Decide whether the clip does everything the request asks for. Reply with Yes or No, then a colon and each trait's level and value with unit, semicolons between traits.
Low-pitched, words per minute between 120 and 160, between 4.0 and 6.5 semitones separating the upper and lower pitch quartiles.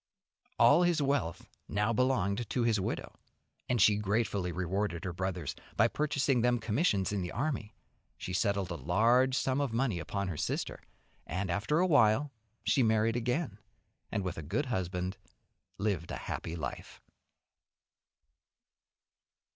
Yes: low, 105 Hz; average, 145 wpm; average, 5.2 semitones